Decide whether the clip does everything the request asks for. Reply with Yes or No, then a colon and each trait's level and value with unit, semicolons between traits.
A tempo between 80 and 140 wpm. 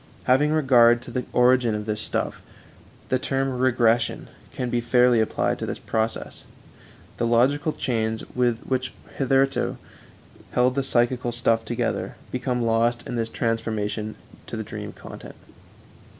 Yes: slow, 135 wpm